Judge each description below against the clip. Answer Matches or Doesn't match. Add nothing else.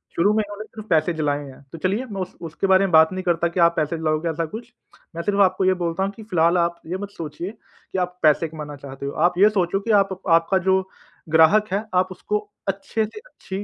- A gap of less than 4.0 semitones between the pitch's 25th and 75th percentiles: Matches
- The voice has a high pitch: Doesn't match